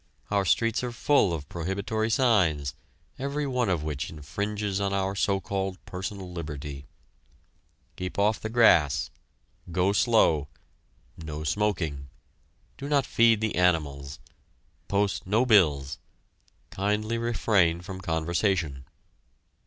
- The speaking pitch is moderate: No, very low, 95 Hz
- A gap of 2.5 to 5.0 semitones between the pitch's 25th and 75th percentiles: No, wide, 5.5 semitones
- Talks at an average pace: No, slow, 115 wpm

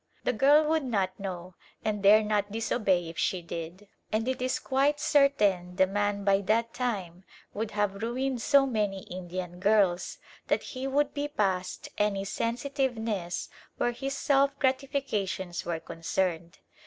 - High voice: Yes, high, 210 Hz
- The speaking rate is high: No, average, 150 wpm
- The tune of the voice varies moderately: No, wide, 5.8 semitones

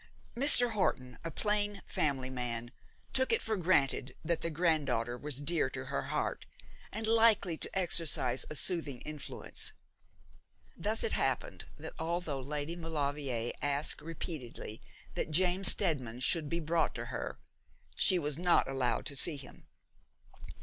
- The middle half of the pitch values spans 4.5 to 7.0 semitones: Yes, average, 4.8 semitones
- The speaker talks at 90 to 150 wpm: Yes, average, 145 wpm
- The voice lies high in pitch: No, medium, 155 Hz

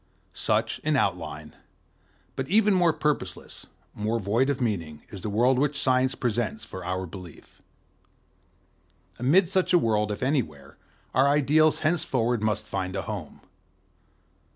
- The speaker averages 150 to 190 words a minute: No, slow, 135 wpm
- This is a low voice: Yes, low, 125 Hz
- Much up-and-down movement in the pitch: Yes, wide, 6.2 semitones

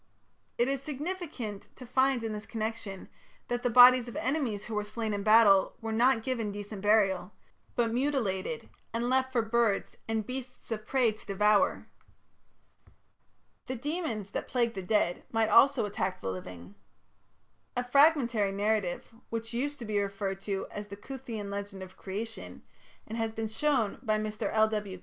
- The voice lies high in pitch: Yes, high, 220 Hz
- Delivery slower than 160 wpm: No, average, 165 wpm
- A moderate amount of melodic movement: Yes, average, 3.3 semitones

